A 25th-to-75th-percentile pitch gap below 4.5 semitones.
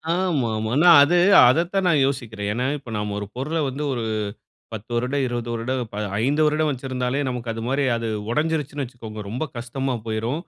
Yes: average, 4.1 semitones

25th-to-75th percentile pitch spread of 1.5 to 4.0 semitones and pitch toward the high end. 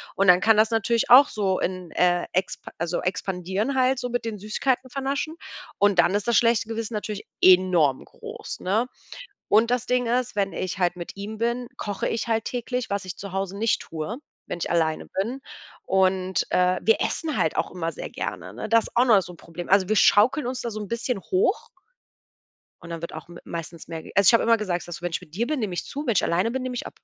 No: average, 4.7 semitones; high, 205 Hz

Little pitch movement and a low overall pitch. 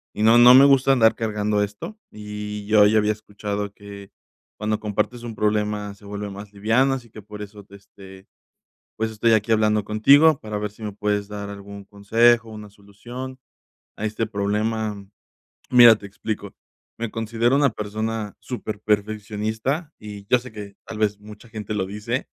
Yes: narrow, 1.6 semitones; low, 105 Hz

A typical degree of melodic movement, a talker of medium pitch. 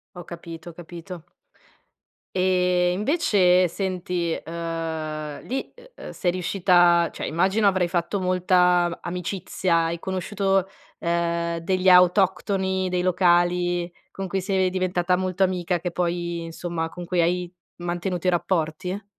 No: narrow, 1.5 semitones; medium, 180 Hz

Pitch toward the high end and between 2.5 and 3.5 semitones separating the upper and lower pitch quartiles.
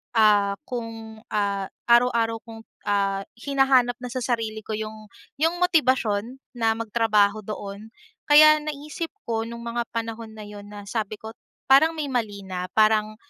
Yes: high, 225 Hz; average, 2.8 semitones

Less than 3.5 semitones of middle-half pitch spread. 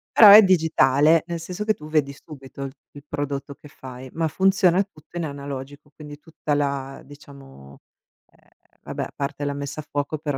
Yes: average, 2.7 semitones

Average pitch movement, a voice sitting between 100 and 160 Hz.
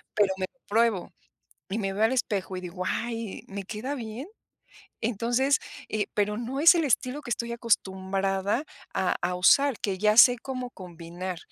No: average, 4.2 semitones; high, 215 Hz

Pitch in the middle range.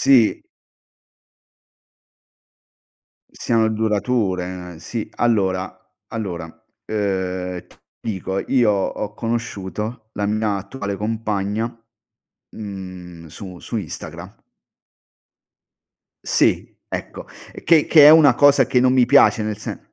No: low, 105 Hz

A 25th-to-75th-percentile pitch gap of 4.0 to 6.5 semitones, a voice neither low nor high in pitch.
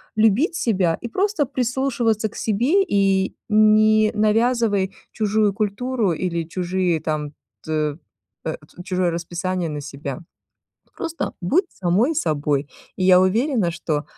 No: average, 5.0 semitones; high, 195 Hz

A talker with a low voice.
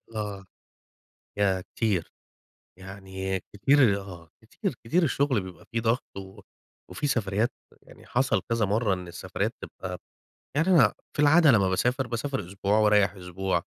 Yes: low, 105 Hz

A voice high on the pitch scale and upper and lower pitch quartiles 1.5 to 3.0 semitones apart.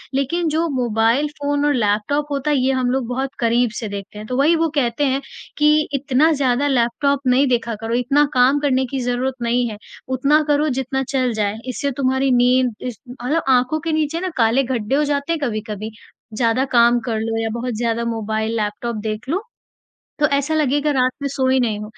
No: very high, 255 Hz; average, 3.5 semitones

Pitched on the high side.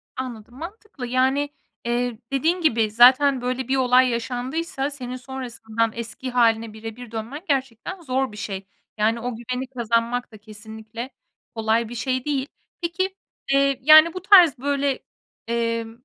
Yes: very high, 250 Hz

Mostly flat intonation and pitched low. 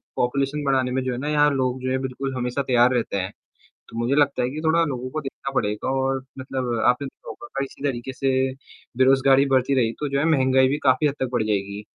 Yes: narrow, 1.8 semitones; low, 130 Hz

